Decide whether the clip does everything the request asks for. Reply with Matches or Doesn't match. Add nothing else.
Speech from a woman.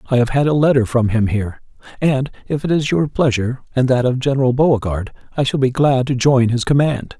Doesn't match